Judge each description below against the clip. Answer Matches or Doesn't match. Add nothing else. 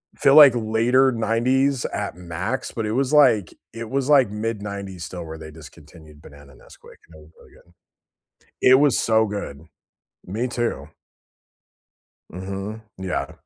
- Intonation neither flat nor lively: Doesn't match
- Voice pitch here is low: Matches